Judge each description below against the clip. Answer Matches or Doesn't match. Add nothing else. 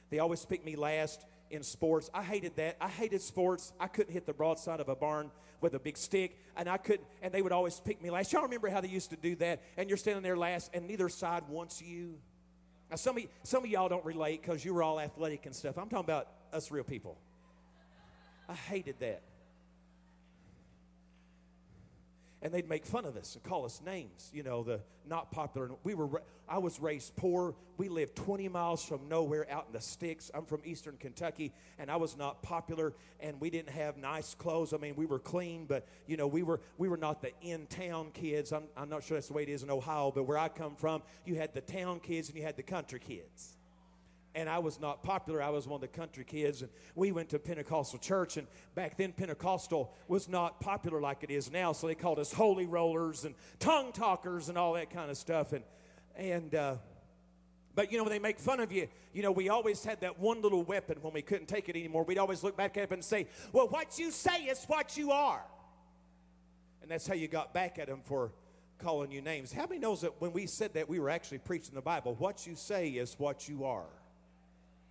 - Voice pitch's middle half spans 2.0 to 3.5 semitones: Doesn't match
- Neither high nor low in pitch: Matches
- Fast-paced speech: Matches